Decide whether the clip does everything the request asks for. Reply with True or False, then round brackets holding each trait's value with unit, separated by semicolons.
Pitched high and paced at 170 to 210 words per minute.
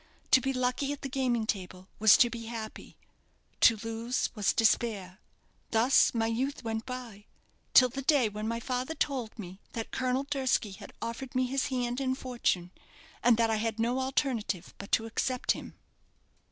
True (235 Hz; 175 wpm)